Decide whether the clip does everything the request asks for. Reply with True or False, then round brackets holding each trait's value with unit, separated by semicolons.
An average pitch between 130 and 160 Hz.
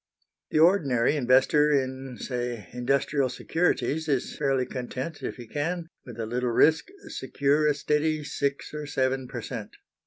True (135 Hz)